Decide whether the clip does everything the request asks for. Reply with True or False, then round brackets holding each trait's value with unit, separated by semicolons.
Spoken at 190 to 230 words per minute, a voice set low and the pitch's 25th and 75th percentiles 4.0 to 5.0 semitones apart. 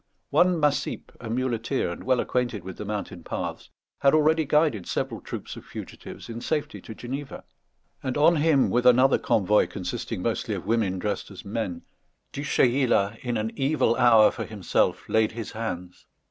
False (170 wpm; 120 Hz; 4.6 semitones)